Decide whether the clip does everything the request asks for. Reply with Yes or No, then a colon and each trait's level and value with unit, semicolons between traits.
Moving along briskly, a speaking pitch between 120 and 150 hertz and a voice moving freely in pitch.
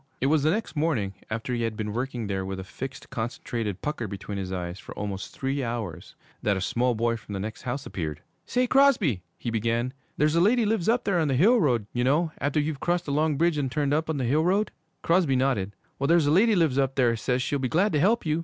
Yes: fast, 250 wpm; low, 135 Hz; wide, 6.0 semitones